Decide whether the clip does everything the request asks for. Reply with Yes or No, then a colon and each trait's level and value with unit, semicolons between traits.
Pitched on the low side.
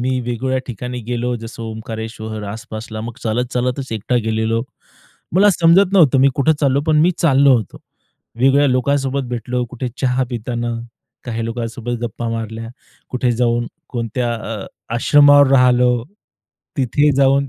Yes: low, 125 Hz